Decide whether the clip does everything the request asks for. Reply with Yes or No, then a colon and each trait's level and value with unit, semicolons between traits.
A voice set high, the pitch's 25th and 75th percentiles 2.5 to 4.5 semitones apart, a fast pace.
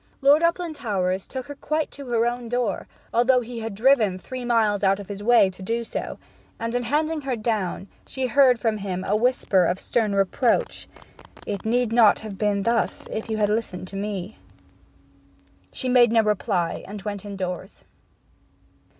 No: high, 225 Hz; average, 3.7 semitones; average, 175 wpm